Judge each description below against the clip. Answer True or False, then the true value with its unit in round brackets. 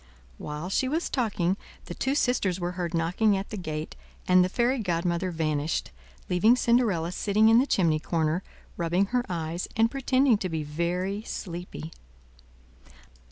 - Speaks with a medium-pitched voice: True (180 Hz)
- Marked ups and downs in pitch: False (4.8 semitones)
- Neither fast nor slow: True (155 wpm)